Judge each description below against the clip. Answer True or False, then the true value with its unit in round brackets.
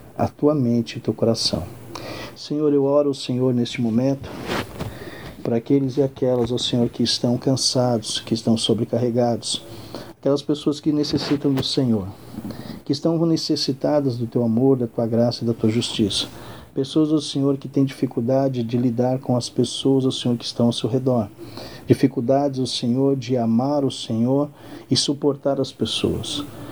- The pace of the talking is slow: False (165 wpm)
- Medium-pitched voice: False (130 Hz)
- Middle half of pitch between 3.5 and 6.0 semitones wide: False (2.8 semitones)